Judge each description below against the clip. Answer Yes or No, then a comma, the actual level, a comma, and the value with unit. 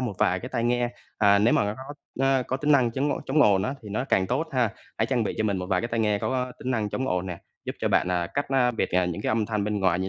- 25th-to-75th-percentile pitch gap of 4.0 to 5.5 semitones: Yes, average, 4.5 semitones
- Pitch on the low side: Yes, low, 115 Hz